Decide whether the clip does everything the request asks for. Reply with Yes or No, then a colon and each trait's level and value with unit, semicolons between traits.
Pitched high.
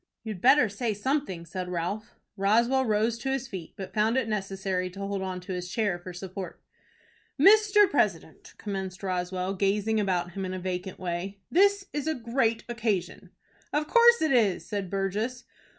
Yes: high, 200 Hz